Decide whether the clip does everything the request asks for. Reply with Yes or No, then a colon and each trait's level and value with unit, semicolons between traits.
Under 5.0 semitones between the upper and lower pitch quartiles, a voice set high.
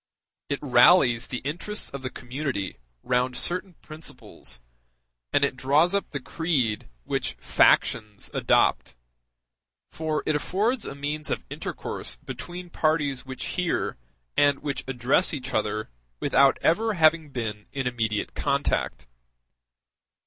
No: average, 4.5 semitones; medium, 140 Hz